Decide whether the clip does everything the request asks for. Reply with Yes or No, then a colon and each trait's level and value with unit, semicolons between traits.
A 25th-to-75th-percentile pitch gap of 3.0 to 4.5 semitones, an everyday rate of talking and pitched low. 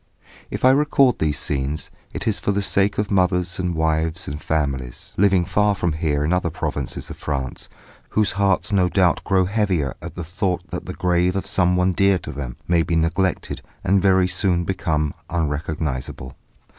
Yes: average, 3.6 semitones; average, 180 wpm; very low, 90 Hz